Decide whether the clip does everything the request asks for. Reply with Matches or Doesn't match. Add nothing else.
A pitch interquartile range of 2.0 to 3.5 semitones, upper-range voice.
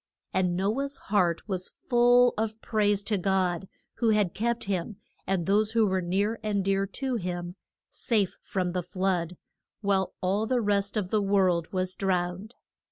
Matches